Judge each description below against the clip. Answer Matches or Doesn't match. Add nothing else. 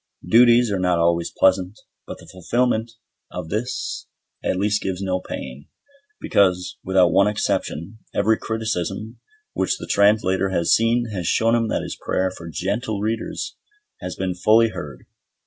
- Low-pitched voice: Matches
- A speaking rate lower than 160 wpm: Matches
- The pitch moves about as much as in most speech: Matches